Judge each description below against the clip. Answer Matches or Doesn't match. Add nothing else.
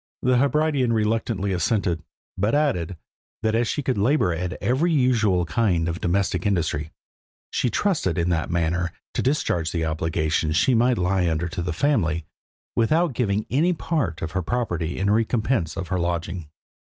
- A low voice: Matches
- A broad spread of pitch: Matches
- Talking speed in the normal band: Matches